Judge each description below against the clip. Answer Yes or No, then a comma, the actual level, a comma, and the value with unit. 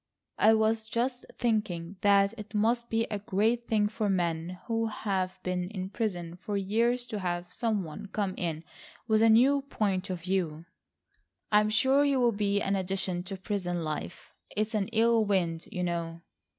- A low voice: No, high, 205 Hz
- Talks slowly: No, average, 175 wpm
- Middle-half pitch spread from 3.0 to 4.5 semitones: Yes, average, 3.6 semitones